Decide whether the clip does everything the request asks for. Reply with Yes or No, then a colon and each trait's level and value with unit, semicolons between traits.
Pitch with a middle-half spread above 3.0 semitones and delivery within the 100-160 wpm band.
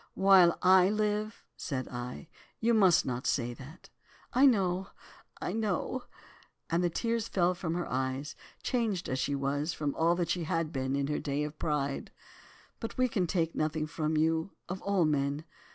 No: average, 5.0 semitones; average, 170 wpm